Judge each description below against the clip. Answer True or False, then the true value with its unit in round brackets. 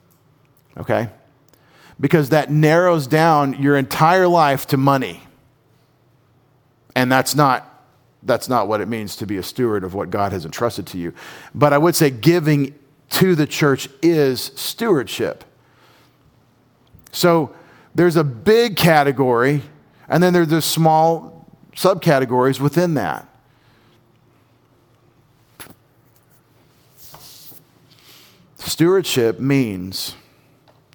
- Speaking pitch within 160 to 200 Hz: False (140 Hz)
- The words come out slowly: True (105 wpm)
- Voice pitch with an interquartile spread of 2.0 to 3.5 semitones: False (4.3 semitones)